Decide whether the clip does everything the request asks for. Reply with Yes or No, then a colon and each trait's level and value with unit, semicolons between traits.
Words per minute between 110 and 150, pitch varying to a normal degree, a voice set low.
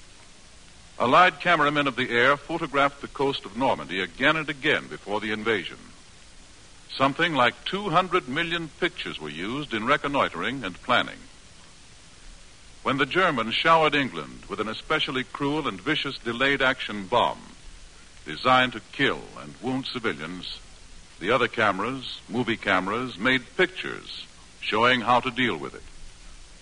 No: slow, 135 wpm; wide, 6.1 semitones; low, 130 Hz